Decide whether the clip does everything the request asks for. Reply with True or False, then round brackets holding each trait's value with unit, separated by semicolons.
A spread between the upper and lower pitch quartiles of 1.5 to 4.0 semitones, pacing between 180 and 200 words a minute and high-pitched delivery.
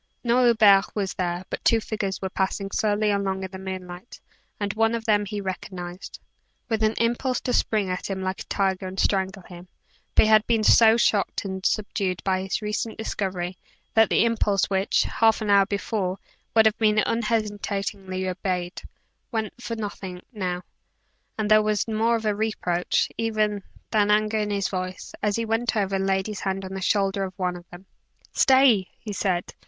True (2.4 semitones; 185 wpm; 200 Hz)